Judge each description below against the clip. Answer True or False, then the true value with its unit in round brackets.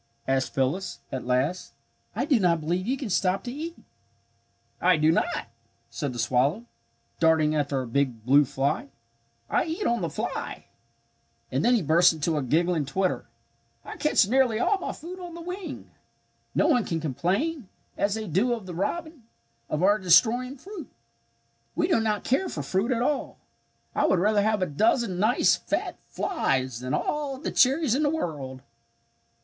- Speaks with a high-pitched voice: True (195 Hz)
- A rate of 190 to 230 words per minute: False (175 wpm)